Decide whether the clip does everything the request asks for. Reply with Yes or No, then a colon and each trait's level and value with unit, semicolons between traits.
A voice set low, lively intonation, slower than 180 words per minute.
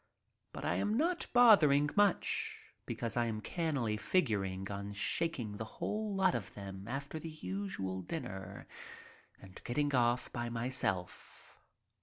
Yes: low, 120 Hz; wide, 8.6 semitones; slow, 135 wpm